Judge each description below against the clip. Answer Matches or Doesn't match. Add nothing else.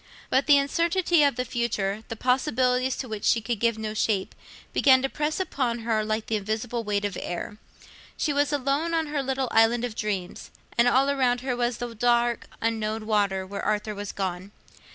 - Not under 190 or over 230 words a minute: Matches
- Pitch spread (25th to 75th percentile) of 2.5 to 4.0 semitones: Matches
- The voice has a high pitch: Matches